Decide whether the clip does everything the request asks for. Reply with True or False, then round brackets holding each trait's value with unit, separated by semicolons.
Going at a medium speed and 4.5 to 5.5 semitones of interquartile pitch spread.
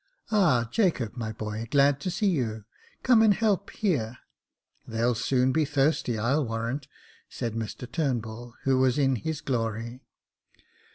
True (160 wpm; 5.2 semitones)